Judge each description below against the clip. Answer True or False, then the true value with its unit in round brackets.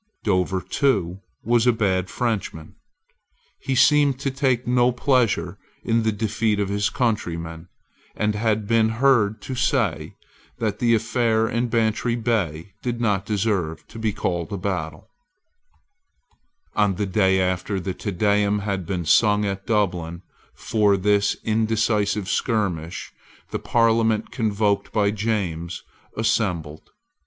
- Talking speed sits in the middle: False (130 wpm)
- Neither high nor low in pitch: False (105 Hz)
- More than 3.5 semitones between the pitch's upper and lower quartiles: False (3.2 semitones)